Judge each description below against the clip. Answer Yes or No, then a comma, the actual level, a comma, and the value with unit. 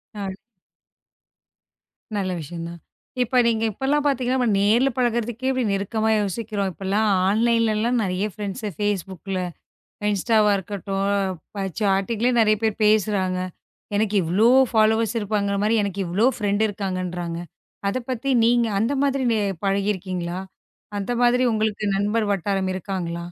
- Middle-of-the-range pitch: No, high, 205 Hz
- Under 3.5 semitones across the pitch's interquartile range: Yes, average, 2.8 semitones